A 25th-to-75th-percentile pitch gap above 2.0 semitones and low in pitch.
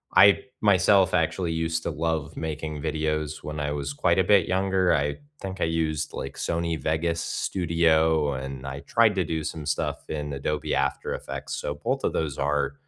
Yes: narrow, 2.5 semitones; very low, 80 Hz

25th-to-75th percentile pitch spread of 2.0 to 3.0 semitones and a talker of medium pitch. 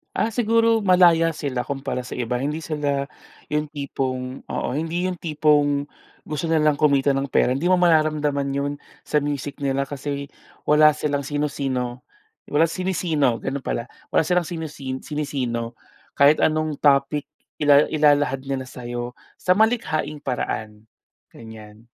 Yes: narrow, 2.5 semitones; medium, 145 Hz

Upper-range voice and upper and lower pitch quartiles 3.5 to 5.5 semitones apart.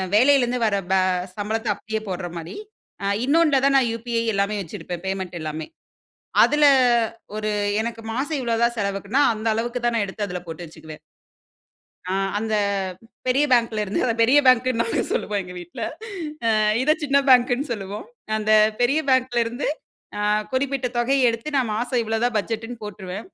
Yes: high, 230 Hz; average, 3.8 semitones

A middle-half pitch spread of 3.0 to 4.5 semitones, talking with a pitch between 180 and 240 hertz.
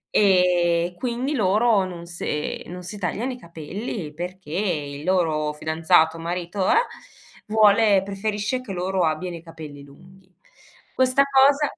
Yes: average, 4.1 semitones; medium, 185 Hz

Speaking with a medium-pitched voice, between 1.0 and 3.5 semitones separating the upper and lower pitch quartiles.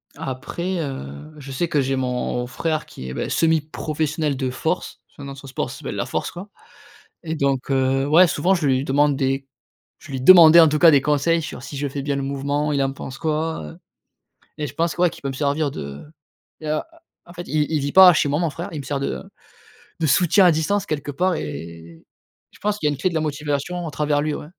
Yes: medium, 145 Hz; average, 2.9 semitones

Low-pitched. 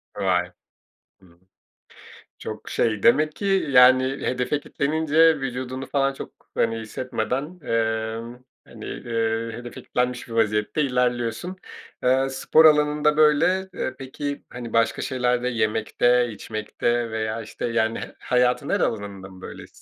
Yes: low, 125 Hz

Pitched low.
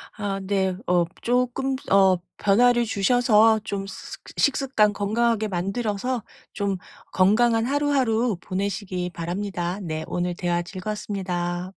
No: high, 200 Hz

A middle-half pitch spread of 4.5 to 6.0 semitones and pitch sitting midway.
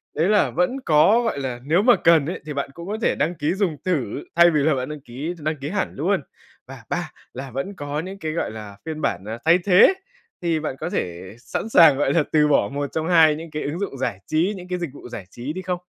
No: average, 4.0 semitones; medium, 155 Hz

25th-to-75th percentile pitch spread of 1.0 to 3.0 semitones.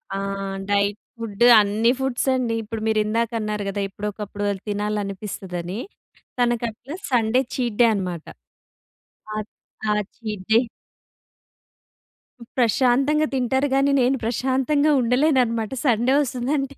No: average, 3.6 semitones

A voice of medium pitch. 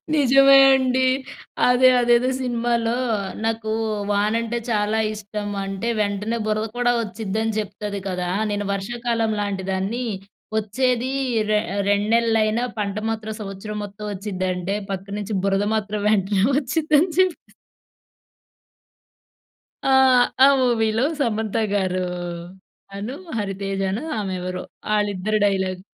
No: high, 215 Hz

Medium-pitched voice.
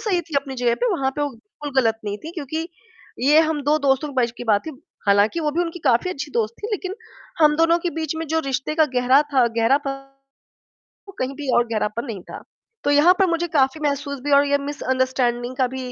No: very high, 280 Hz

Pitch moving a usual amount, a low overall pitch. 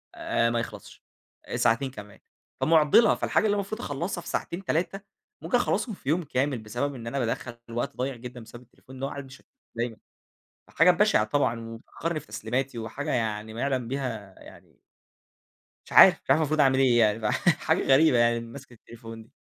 Yes: average, 4.1 semitones; low, 125 Hz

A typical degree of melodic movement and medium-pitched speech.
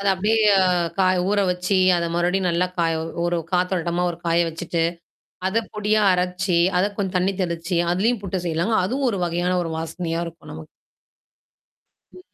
No: narrow, 2.3 semitones; medium, 180 Hz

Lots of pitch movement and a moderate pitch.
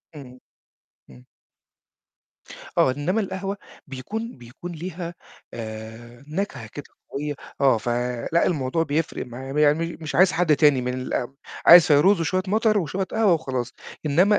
Yes: wide, 5.8 semitones; medium, 150 Hz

